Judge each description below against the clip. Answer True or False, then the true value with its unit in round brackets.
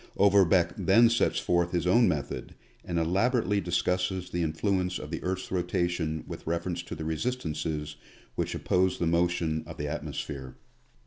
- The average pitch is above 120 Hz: False (90 Hz)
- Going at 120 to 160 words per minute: True (155 wpm)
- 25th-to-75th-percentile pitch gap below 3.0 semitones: True (2.6 semitones)